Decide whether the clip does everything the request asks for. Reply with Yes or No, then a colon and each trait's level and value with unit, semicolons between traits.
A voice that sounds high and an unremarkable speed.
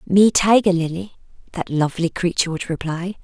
No: medium, 180 Hz; average, 150 wpm